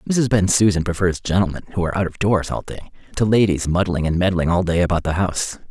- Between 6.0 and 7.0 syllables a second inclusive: Yes, 6.6 syllables/s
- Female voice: No, male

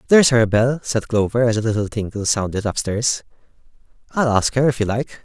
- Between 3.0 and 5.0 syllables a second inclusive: No, 5.8 syllables/s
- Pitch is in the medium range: No, low, 115 Hz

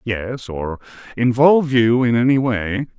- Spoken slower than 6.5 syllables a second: Yes, 4.1 syllables/s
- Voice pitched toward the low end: Yes, low, 120 Hz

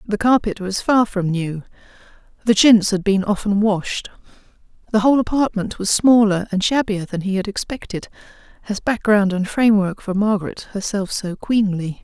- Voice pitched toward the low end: No, high, 205 Hz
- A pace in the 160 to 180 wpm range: Yes, average, 170 wpm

